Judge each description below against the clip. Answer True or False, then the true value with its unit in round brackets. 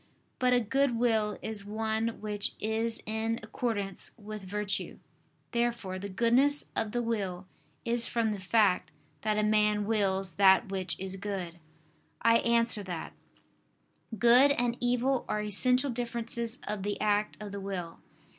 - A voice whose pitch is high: True (215 Hz)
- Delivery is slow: False (145 wpm)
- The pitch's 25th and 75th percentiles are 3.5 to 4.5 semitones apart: False (2.7 semitones)